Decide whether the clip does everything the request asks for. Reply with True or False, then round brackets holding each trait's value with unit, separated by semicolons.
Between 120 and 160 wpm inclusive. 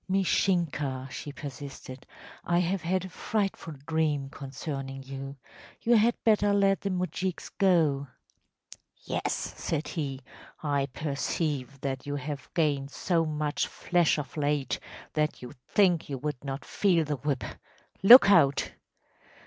True (135 wpm)